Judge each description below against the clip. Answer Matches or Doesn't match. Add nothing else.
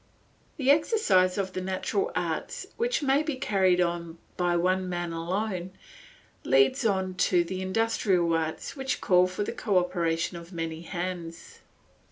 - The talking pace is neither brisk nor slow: Matches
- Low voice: Doesn't match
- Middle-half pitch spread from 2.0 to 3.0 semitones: Doesn't match